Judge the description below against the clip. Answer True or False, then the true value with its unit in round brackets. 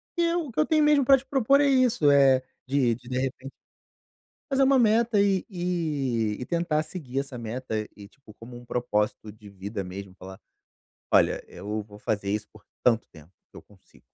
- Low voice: True (130 Hz)